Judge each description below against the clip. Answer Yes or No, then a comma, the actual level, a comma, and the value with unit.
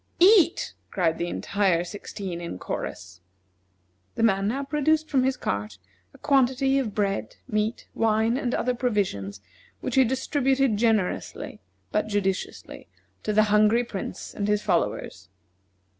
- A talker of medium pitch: No, high, 215 Hz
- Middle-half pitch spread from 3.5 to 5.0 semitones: No, wide, 5.4 semitones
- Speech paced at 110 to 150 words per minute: Yes, slow, 135 wpm